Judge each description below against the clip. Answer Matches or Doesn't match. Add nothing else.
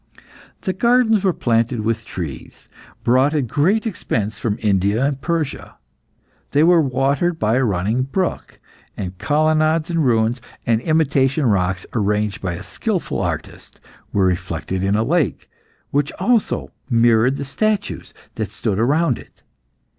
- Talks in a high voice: Doesn't match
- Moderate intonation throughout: Doesn't match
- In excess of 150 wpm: Doesn't match